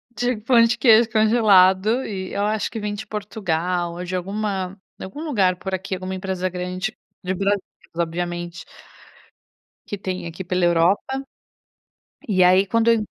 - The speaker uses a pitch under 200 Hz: Yes, high, 190 Hz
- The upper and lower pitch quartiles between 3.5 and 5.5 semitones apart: No, average, 3.0 semitones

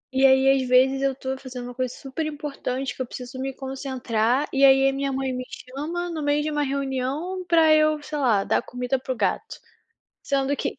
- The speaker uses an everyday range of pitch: No, narrow, 2.0 semitones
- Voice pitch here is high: Yes, very high, 270 Hz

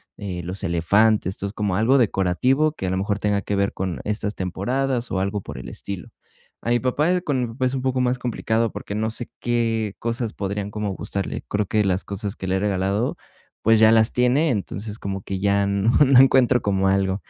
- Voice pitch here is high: No, low, 105 Hz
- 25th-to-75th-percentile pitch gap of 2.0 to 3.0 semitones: No, average, 3.6 semitones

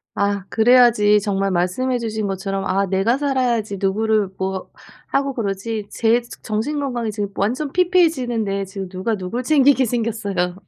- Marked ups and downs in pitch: No, average, 4.0 semitones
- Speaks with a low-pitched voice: No, high, 220 Hz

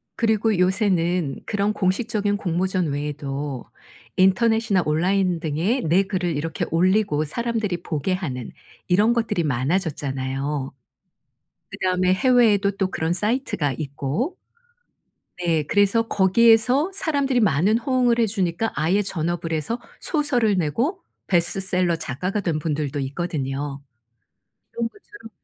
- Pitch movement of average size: No, wide, 6.0 semitones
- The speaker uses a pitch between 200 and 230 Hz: No, medium, 185 Hz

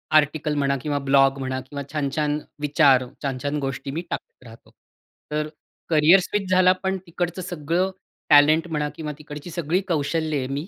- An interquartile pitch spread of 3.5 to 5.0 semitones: No, average, 2.9 semitones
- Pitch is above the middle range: No, medium, 150 Hz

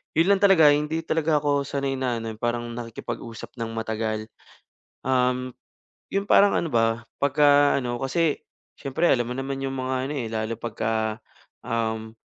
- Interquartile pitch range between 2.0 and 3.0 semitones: No, average, 4.2 semitones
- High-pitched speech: No, low, 130 Hz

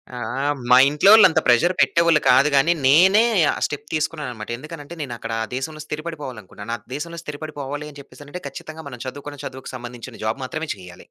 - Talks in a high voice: No, medium, 145 Hz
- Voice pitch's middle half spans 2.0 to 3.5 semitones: No, average, 3.9 semitones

